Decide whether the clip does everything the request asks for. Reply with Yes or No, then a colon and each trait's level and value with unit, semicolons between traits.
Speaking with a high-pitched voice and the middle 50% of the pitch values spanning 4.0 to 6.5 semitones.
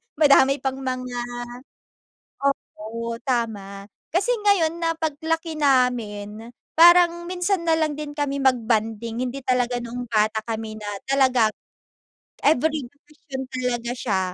Yes: very high, 255 Hz; average, 4.9 semitones